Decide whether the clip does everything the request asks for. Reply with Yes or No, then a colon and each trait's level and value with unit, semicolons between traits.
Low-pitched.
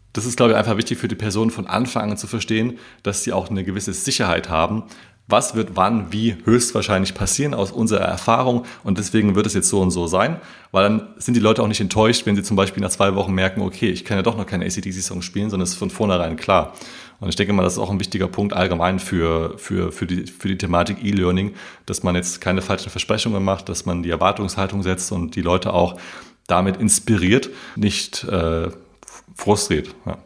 Yes: low, 100 Hz